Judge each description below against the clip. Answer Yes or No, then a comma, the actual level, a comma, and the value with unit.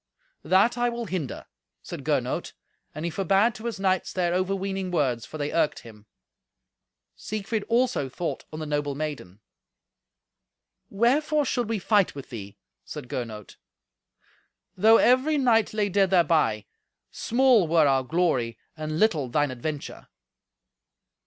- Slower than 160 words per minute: Yes, slow, 135 wpm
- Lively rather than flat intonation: Yes, wide, 7.1 semitones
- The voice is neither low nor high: Yes, medium, 180 Hz